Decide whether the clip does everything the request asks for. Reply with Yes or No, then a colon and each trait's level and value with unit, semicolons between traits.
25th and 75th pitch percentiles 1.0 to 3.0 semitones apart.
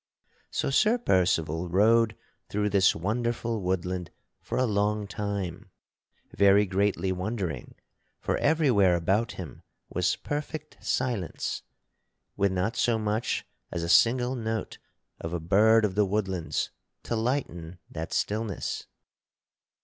No: average, 3.9 semitones